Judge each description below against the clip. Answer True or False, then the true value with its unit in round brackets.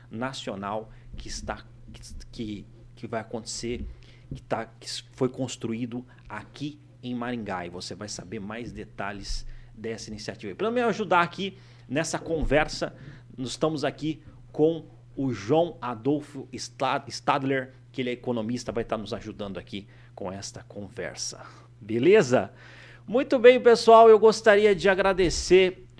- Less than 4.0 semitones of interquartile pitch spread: False (4.4 semitones)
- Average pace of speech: True (130 wpm)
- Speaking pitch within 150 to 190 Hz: False (125 Hz)